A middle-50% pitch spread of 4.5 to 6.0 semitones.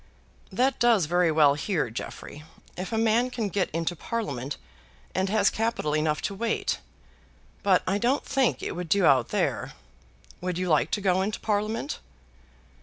Yes: wide, 5.6 semitones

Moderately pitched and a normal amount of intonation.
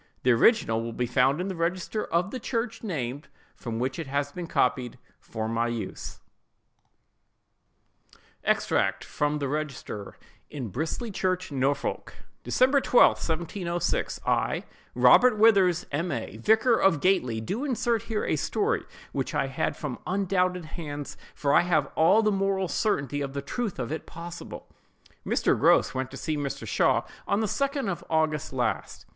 No: medium, 165 Hz; wide, 6.2 semitones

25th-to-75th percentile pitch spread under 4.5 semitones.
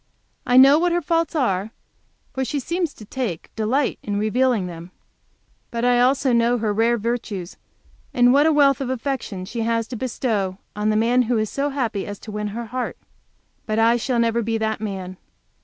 Yes: average, 3.4 semitones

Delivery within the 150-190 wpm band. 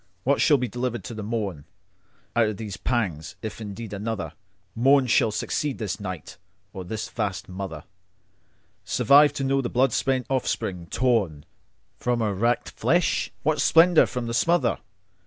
No: average, 140 wpm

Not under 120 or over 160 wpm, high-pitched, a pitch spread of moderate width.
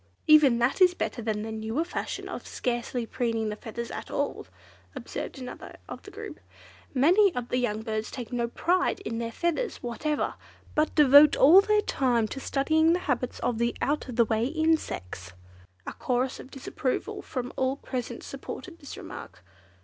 No: average, 170 wpm; very high, 255 Hz; average, 4.7 semitones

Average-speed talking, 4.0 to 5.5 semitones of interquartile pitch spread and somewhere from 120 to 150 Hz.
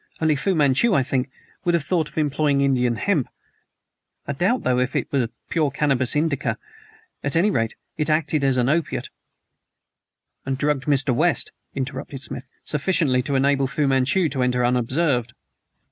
No: average, 165 wpm; average, 3.1 semitones; medium, 140 Hz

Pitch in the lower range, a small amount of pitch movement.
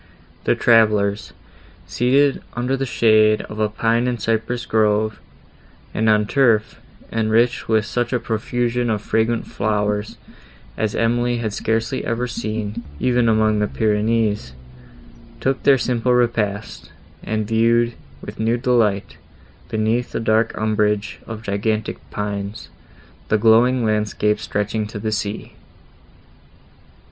Yes: low, 110 Hz; narrow, 1.9 semitones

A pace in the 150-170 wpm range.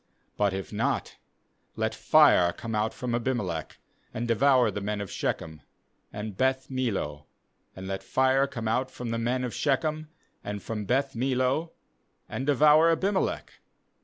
Yes: average, 155 wpm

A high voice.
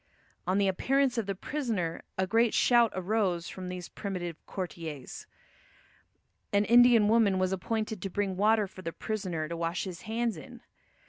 Yes: high, 195 Hz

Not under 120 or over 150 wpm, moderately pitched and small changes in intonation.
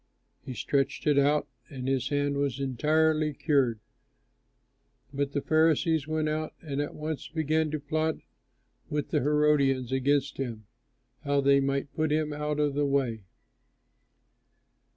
Yes: average, 140 wpm; medium, 145 Hz; narrow, 1.9 semitones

